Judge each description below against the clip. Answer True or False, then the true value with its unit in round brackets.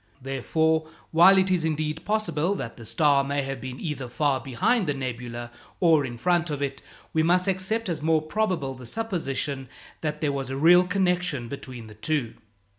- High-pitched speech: False (150 Hz)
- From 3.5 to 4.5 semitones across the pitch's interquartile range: False (5.0 semitones)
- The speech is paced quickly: False (185 wpm)